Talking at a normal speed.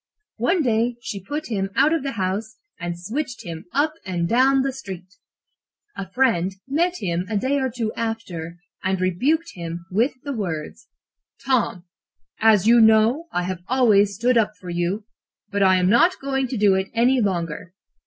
Yes: average, 175 wpm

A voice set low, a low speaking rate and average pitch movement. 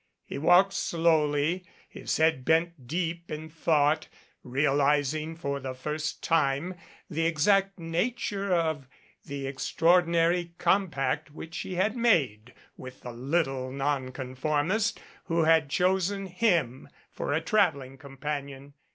No: medium, 155 Hz; slow, 115 wpm; average, 3.8 semitones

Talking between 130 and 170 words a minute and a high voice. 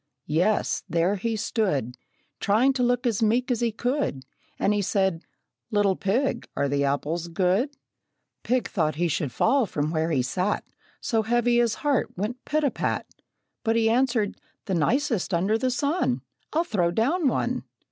Yes: average, 165 wpm; high, 215 Hz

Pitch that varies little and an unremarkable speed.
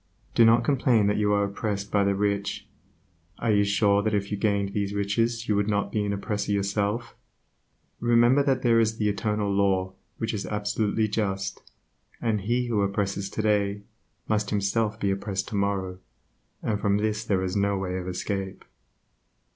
Yes: narrow, 1.5 semitones; average, 170 wpm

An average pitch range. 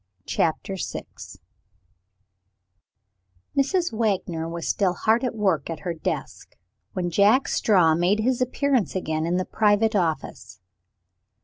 Yes: average, 5.0 semitones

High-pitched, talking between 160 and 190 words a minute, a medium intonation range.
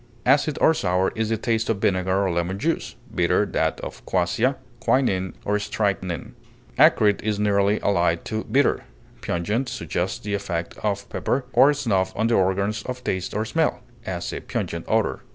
No: low, 100 Hz; average, 170 wpm; average, 3.3 semitones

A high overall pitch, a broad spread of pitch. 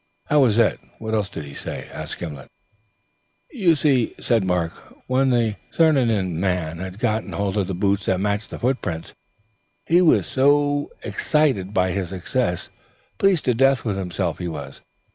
No: low, 105 Hz; wide, 6.4 semitones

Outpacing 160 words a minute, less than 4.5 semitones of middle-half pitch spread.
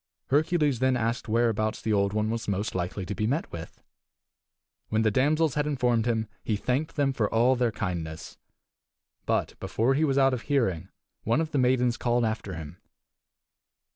Yes: average, 175 wpm; average, 4.0 semitones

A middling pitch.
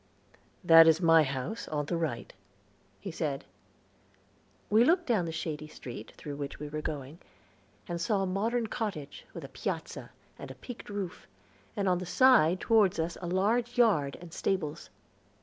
Yes: medium, 175 Hz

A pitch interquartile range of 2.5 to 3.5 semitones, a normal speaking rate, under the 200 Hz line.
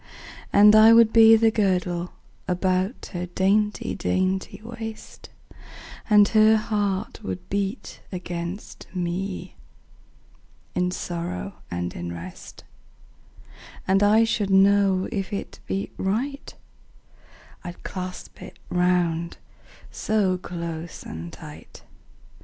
No: average, 2.9 semitones; slow, 105 wpm; high, 190 Hz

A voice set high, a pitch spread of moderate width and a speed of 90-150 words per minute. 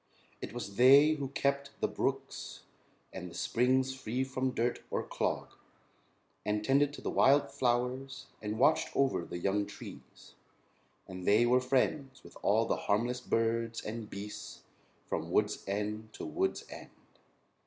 No: low, 120 Hz; average, 4.0 semitones; average, 145 wpm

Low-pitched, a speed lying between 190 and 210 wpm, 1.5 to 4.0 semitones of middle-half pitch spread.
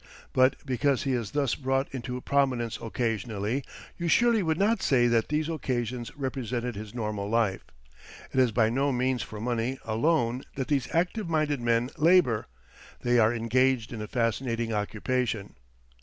No: low, 125 Hz; average, 155 wpm; average, 3.2 semitones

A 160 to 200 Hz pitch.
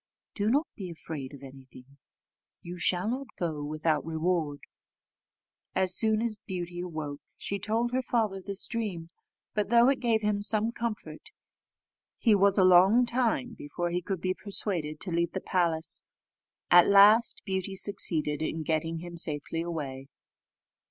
Yes: medium, 185 Hz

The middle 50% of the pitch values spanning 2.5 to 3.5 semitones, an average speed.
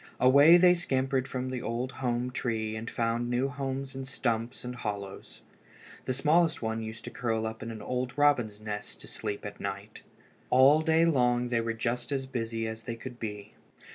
Yes: average, 2.9 semitones; average, 190 wpm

